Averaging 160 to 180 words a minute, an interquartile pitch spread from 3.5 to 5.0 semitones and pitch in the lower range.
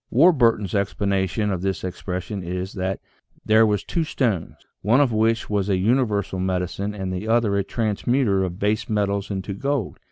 No: average, 165 wpm; average, 2.9 semitones; low, 100 Hz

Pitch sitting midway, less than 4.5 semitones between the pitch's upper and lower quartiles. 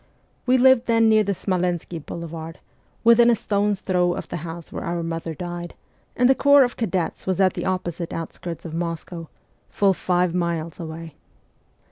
Yes: medium, 175 Hz; average, 3.7 semitones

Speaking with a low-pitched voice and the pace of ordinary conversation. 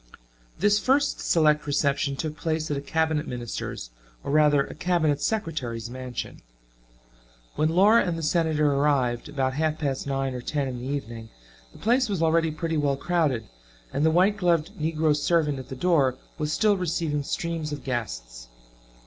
No: medium, 150 Hz; average, 165 wpm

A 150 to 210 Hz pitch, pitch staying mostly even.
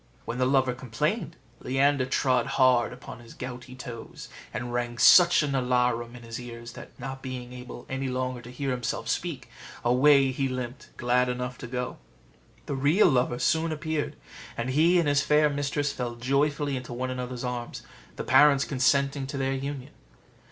No: low, 130 Hz; narrow, 2.3 semitones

